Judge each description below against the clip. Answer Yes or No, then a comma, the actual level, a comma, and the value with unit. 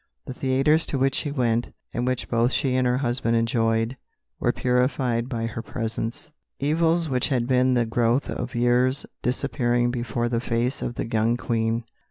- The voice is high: No, low, 120 Hz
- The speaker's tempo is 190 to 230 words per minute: No, average, 175 wpm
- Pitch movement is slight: Yes, narrow, 1.9 semitones